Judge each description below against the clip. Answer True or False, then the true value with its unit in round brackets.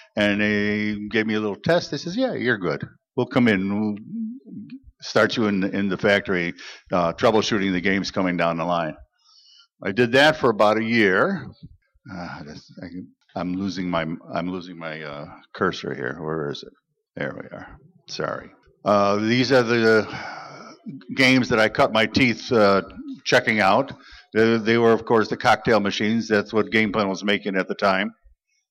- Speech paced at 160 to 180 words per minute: True (175 wpm)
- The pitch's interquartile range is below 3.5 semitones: False (4.3 semitones)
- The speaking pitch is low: True (105 Hz)